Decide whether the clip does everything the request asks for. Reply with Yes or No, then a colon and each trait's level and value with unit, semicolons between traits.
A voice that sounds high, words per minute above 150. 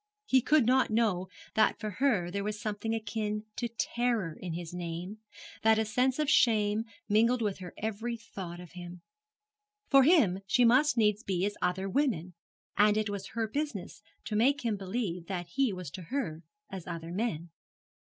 Yes: high, 210 Hz; average, 180 wpm